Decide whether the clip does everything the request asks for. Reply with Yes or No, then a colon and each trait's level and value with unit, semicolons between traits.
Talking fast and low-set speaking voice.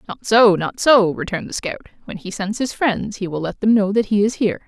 No: fast, 270 wpm; high, 205 Hz